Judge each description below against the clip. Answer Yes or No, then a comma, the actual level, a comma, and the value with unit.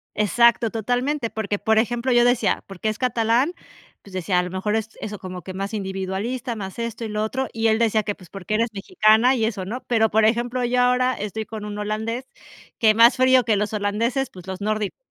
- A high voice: Yes, high, 220 Hz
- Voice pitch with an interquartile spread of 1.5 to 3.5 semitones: Yes, average, 2.7 semitones